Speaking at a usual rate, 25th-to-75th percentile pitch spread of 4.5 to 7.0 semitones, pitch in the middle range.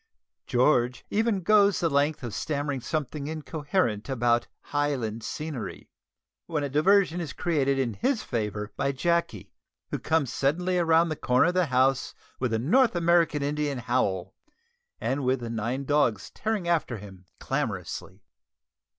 Yes: average, 145 wpm; wide, 5.5 semitones; medium, 145 Hz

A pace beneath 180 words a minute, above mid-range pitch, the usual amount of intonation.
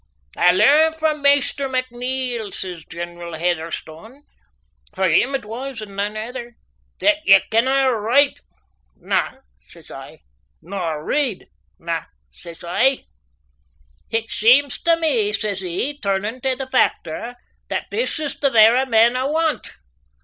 No: slow, 135 wpm; high, 235 Hz; wide, 5.9 semitones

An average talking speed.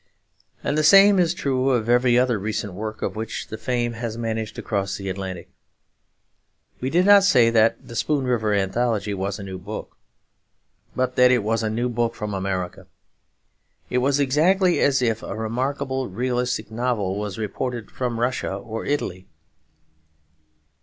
Yes: average, 165 wpm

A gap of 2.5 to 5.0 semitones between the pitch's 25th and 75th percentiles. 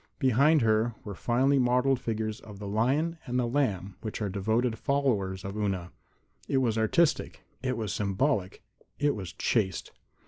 Yes: average, 4.5 semitones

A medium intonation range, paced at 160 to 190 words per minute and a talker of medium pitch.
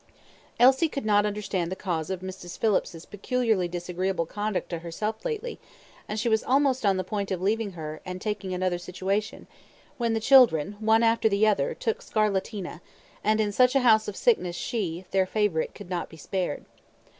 No: average, 3.4 semitones; average, 180 wpm; high, 205 Hz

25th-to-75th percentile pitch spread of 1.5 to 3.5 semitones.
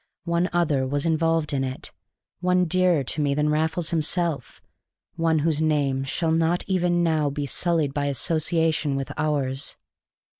Yes: average, 2.9 semitones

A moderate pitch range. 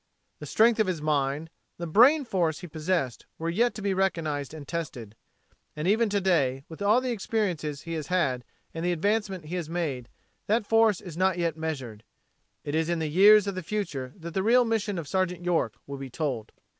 Yes: average, 4.9 semitones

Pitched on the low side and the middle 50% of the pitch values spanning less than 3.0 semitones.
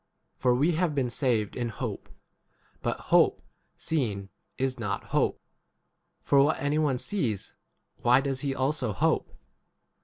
No: low, 130 Hz; average, 3.6 semitones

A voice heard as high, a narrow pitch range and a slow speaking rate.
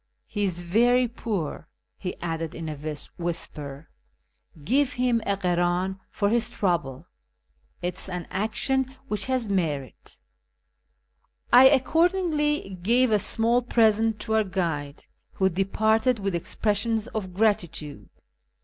No: high, 200 Hz; average, 5.3 semitones; slow, 125 wpm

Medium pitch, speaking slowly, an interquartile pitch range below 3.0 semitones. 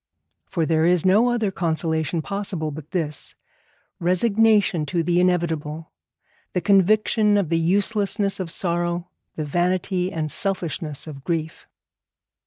No: medium, 175 Hz; slow, 125 wpm; average, 3.5 semitones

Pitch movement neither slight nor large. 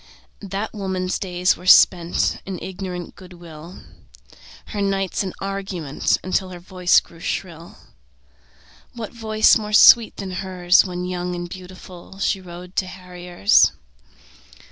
No: narrow, 1.6 semitones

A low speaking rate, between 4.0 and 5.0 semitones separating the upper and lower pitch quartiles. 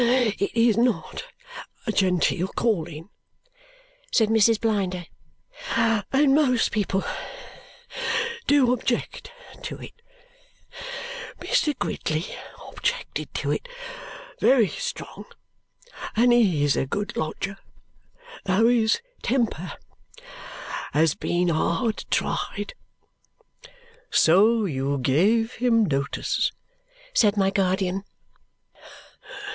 Yes: slow, 90 wpm; average, 4.7 semitones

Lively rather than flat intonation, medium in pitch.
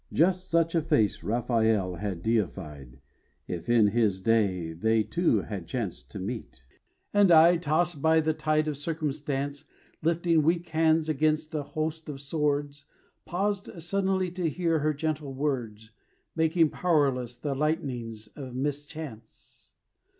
Yes: wide, 6.2 semitones; medium, 145 Hz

